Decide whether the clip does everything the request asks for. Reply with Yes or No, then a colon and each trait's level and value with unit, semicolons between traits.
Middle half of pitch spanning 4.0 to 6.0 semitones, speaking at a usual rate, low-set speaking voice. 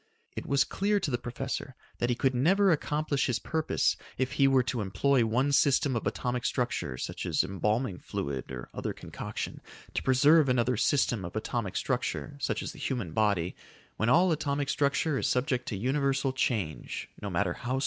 Yes: average, 4.3 semitones; average, 185 wpm; low, 125 Hz